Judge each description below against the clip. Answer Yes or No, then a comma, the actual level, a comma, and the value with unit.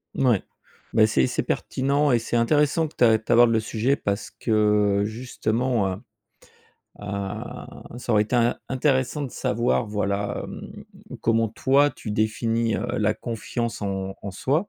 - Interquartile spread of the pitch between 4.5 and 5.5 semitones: No, average, 3.2 semitones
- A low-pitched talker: Yes, low, 115 Hz